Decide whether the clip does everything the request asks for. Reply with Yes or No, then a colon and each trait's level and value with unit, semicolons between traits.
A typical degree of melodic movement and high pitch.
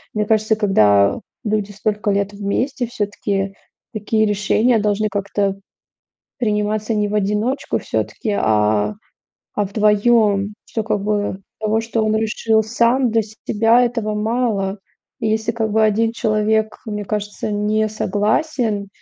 No: narrow, 1.4 semitones; high, 215 Hz